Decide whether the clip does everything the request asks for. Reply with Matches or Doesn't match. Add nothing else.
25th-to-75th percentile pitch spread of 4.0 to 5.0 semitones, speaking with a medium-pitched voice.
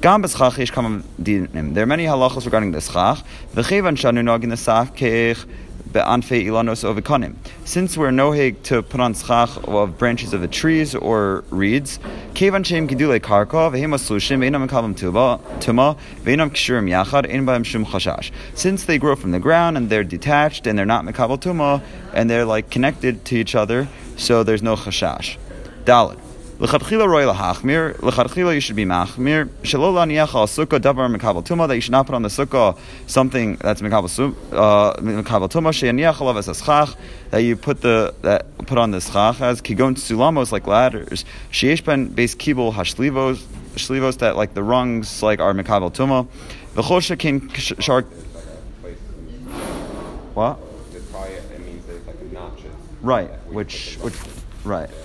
Doesn't match